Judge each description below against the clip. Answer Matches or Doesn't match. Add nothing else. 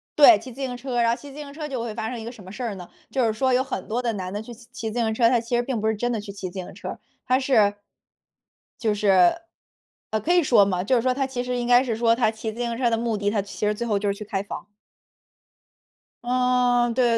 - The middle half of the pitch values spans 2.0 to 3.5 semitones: Matches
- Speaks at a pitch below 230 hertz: Doesn't match